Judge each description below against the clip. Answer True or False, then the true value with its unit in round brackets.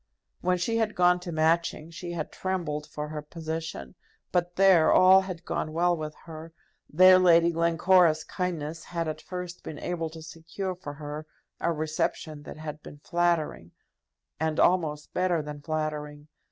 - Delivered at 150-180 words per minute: True (160 wpm)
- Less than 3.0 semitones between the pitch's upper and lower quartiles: True (2.4 semitones)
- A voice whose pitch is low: False (165 Hz)